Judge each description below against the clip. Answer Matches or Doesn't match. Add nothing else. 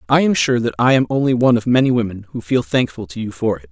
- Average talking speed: Doesn't match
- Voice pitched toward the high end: Doesn't match